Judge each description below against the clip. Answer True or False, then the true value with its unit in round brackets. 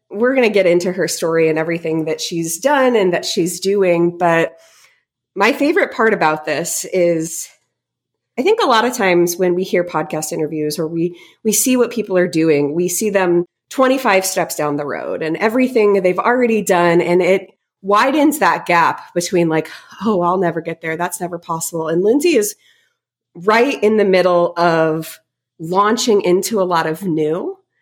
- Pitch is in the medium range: True (180 Hz)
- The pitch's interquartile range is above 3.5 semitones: True (4.5 semitones)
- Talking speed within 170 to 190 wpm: True (180 wpm)